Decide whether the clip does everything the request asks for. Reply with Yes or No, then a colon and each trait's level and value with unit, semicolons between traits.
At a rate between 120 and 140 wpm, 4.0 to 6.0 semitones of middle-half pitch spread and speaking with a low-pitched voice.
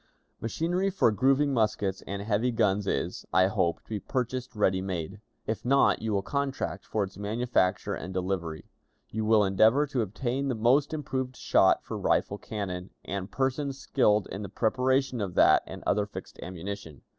No: average, 170 wpm; average, 4.9 semitones; low, 110 Hz